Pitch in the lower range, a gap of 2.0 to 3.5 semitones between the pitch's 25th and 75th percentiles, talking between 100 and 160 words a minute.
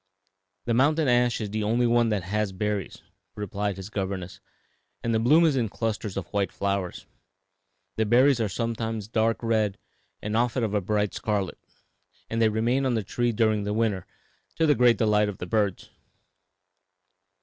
No: low, 110 Hz; narrow, 2.5 semitones; average, 170 wpm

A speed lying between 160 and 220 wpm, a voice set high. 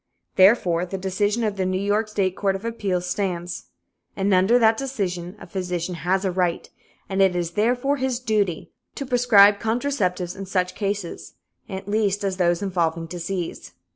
Yes: average, 170 wpm; high, 195 Hz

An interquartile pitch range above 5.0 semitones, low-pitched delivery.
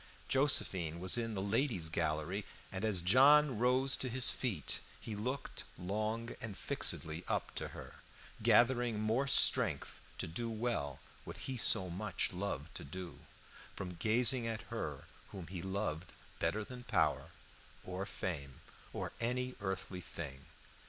Yes: wide, 5.4 semitones; low, 105 Hz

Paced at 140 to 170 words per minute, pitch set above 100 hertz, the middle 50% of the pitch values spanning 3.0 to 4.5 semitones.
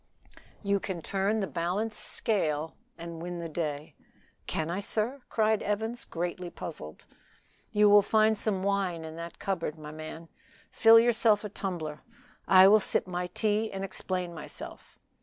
Yes: average, 155 wpm; high, 190 Hz; average, 3.9 semitones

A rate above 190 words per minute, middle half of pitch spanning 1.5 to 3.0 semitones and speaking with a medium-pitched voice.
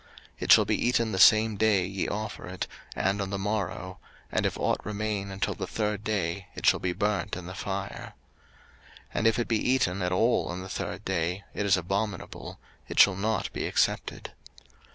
No: average, 200 wpm; narrow, 2.6 semitones; low, 100 Hz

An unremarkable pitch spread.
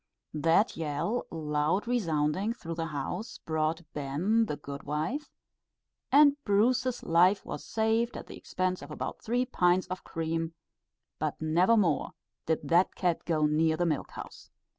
No: wide, 5.9 semitones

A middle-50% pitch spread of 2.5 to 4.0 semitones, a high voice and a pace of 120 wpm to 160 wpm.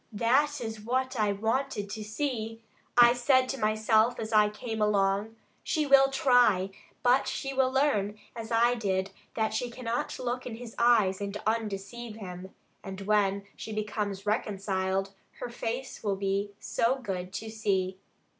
Yes: average, 3.3 semitones; high, 220 Hz; average, 155 wpm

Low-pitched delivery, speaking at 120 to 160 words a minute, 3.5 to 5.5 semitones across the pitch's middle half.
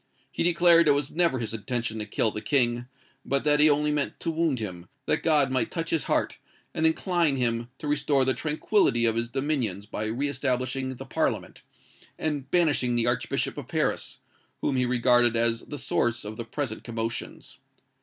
No: low, 130 Hz; average, 185 wpm; average, 4.1 semitones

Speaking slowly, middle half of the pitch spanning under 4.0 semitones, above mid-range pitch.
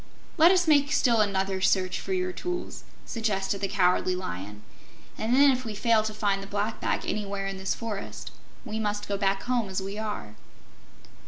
No: average, 185 wpm; average, 2.8 semitones; high, 205 Hz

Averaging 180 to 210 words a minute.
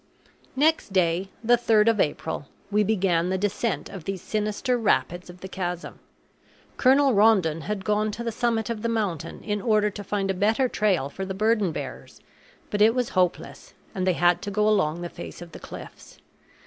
Yes: average, 190 wpm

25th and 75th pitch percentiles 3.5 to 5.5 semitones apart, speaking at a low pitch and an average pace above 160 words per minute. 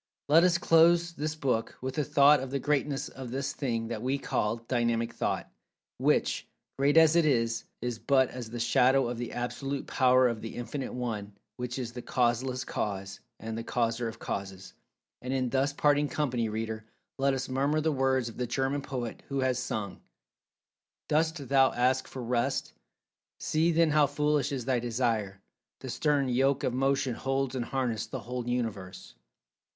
No: average, 2.9 semitones; low, 130 Hz; average, 175 wpm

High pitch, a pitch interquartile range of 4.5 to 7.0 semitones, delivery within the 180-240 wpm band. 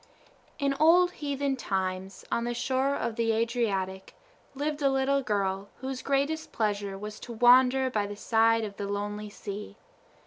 No: high, 230 Hz; average, 4.9 semitones; average, 160 wpm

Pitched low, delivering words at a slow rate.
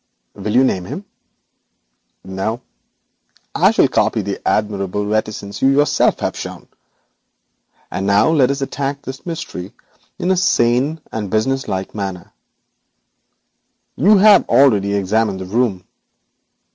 Yes: low, 110 Hz; slow, 120 wpm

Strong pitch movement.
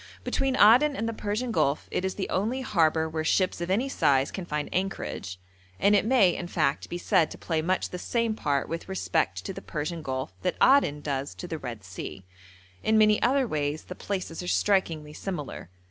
Yes: wide, 5.8 semitones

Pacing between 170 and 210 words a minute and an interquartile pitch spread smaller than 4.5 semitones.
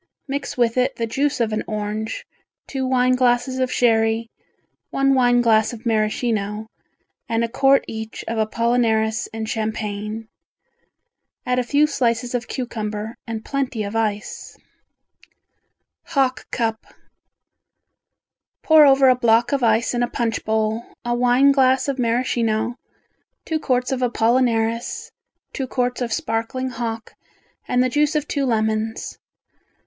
No: slow, 135 wpm; narrow, 2.5 semitones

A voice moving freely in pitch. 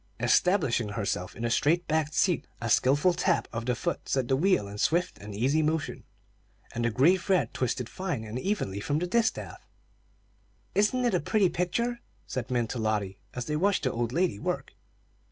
Yes: wide, 7.5 semitones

